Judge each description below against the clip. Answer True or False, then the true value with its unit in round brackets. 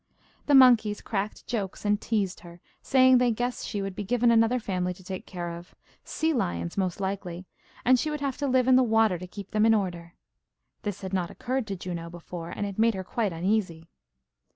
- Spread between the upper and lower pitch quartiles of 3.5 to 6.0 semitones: True (4.7 semitones)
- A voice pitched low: False (205 Hz)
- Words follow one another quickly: True (210 wpm)